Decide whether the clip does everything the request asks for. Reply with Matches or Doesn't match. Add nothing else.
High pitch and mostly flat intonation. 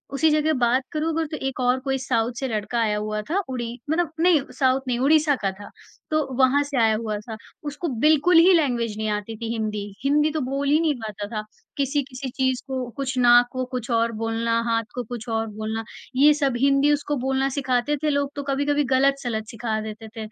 Doesn't match